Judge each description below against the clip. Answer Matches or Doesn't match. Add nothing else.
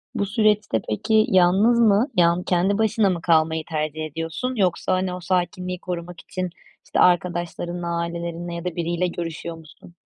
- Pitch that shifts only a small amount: Matches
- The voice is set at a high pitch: Doesn't match